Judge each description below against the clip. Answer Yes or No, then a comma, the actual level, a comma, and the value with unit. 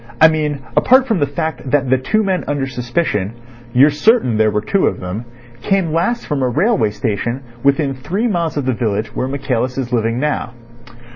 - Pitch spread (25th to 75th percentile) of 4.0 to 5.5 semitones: Yes, average, 5.1 semitones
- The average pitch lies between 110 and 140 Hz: Yes, low, 135 Hz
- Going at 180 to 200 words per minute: Yes, average, 185 wpm